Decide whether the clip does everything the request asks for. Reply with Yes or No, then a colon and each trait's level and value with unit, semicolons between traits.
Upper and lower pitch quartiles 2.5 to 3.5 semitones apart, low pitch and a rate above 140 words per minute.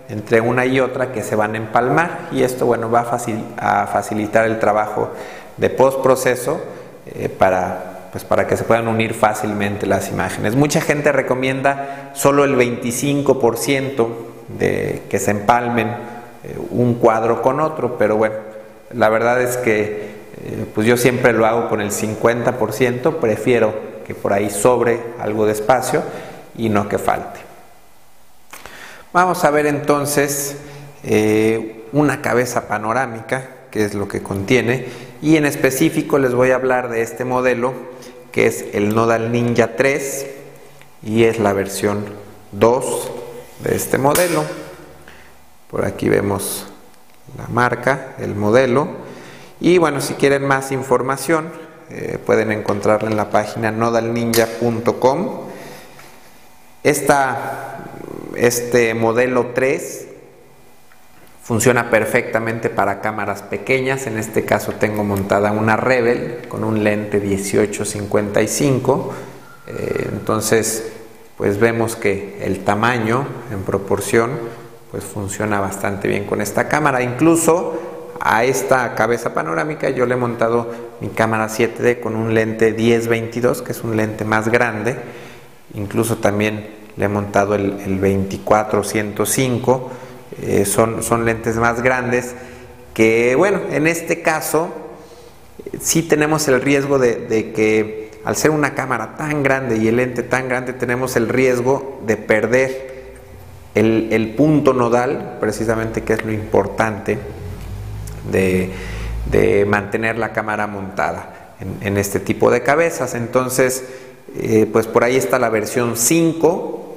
No: average, 3.2 semitones; low, 115 Hz; average, 135 wpm